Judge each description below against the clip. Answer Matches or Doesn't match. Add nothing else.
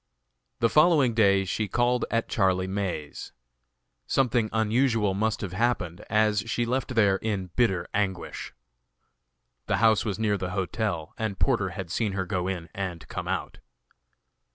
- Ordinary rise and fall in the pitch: Matches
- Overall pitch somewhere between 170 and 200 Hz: Doesn't match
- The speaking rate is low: Doesn't match